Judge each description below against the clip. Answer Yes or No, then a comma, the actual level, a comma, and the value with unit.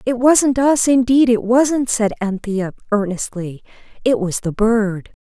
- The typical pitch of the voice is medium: No, high, 225 Hz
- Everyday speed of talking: Yes, average, 150 wpm